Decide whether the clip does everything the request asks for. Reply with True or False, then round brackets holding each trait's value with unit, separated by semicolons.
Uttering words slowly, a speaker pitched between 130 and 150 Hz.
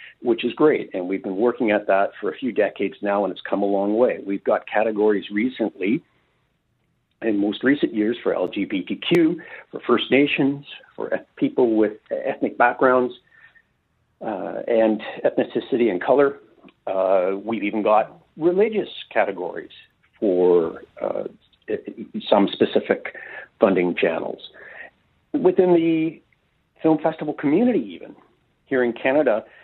True (130 wpm; 140 Hz)